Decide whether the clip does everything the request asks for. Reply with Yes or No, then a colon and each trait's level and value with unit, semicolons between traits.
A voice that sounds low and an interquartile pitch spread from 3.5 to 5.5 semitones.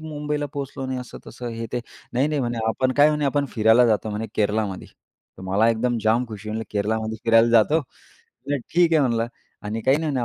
Yes: low, 120 Hz; average, 4.2 semitones